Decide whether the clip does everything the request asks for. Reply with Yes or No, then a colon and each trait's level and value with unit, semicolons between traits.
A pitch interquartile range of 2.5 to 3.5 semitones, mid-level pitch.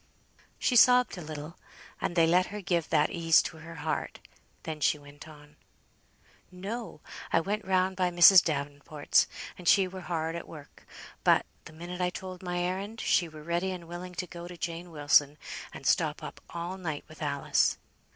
Yes: average, 2.8 semitones; medium, 170 Hz